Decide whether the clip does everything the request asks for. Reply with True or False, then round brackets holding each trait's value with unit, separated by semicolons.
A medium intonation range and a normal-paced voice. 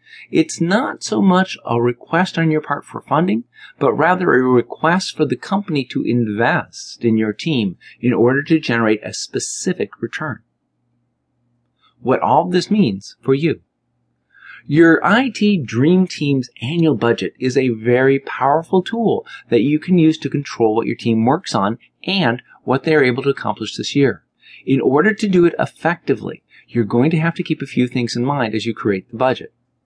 False (5.8 semitones; 180 wpm)